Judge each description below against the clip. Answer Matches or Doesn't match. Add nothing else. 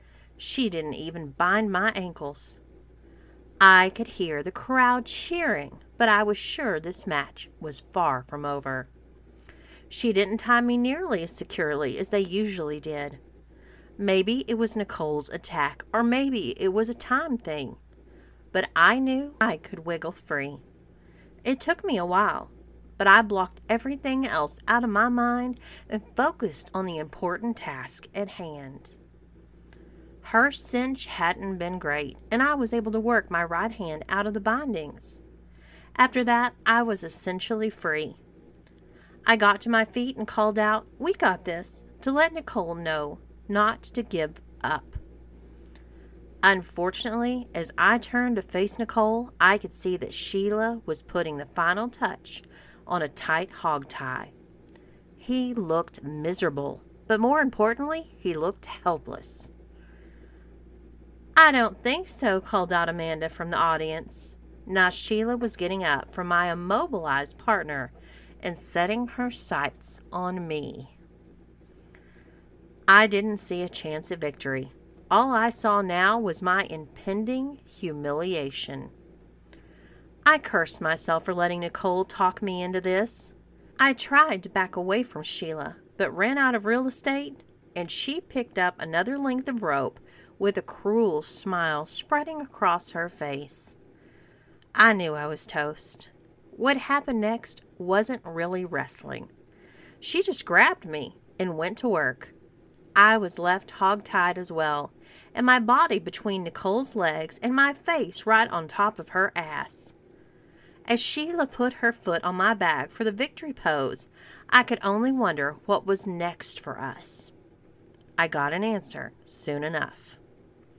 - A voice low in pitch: Doesn't match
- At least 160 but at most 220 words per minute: Doesn't match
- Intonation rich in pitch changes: Matches